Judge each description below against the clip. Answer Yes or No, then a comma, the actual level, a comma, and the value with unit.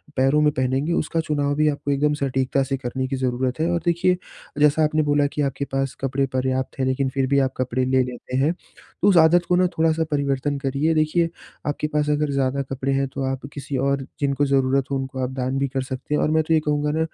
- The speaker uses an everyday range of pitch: No, narrow, 2.3 semitones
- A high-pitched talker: No, medium, 140 Hz